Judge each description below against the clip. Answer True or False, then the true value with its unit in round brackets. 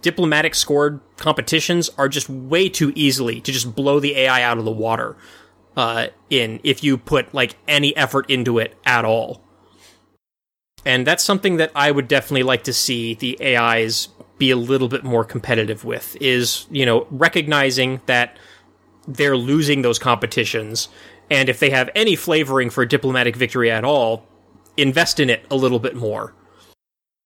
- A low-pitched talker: True (130 Hz)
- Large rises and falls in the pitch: False (3.5 semitones)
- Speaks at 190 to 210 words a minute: False (165 wpm)